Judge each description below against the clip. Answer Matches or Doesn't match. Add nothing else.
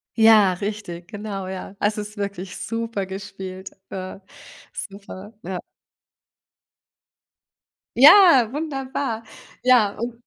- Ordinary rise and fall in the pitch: Matches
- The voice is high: Matches